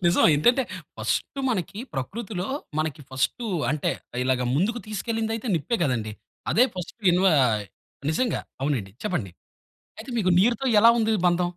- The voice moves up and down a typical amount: No, wide, 7.5 semitones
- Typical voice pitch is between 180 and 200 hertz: Yes, medium, 185 Hz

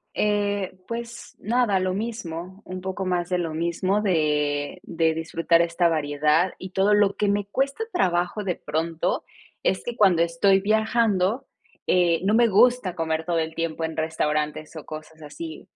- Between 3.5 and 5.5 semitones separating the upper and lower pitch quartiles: Yes, average, 4.0 semitones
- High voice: No, medium, 180 Hz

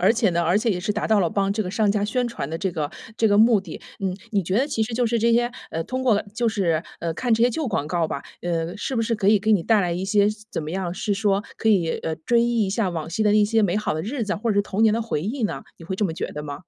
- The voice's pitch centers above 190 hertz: Yes, high, 205 Hz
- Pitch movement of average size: Yes, average, 4.2 semitones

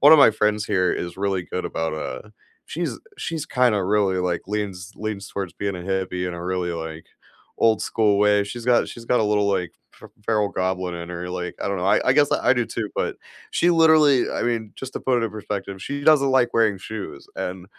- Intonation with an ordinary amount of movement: Yes, average, 4.1 semitones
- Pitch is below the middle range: Yes, low, 100 Hz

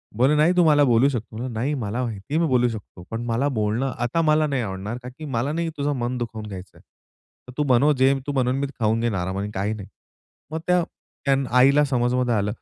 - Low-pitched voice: Yes, low, 125 Hz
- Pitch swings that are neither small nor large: Yes, average, 4.3 semitones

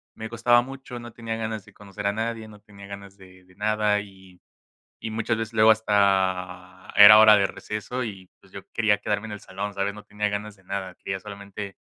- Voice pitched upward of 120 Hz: No, low, 105 Hz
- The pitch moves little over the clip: Yes, narrow, 2.0 semitones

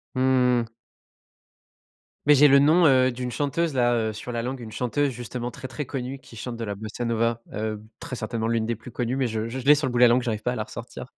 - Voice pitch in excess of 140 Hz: No, low, 125 Hz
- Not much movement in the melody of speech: Yes, narrow, 2.3 semitones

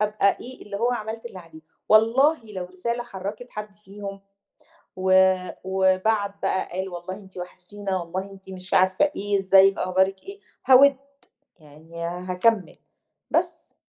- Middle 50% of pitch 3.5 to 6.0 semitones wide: No, average, 2.7 semitones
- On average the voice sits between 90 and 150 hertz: No, high, 195 Hz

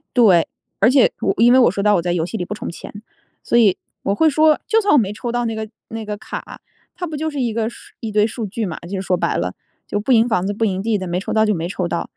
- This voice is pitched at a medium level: No, high, 215 Hz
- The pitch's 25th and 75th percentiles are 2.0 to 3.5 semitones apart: No, average, 4.1 semitones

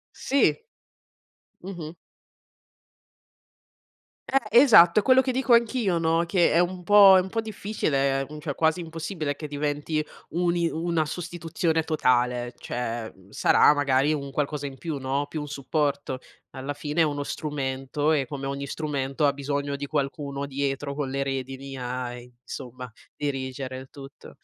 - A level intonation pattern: No, average, 3.5 semitones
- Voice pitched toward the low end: No, medium, 145 Hz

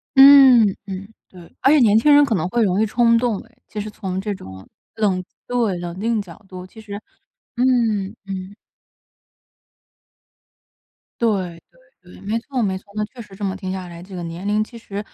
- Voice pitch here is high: Yes, high, 205 Hz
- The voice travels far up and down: No, average, 3.6 semitones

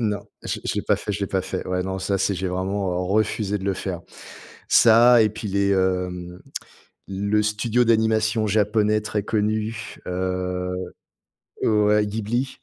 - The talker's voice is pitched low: Yes, low, 105 Hz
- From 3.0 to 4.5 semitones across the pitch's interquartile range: No, narrow, 2.5 semitones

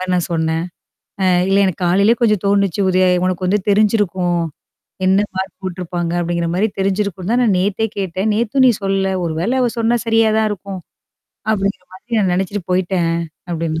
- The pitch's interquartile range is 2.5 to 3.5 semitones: Yes, average, 2.8 semitones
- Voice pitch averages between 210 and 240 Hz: No, high, 190 Hz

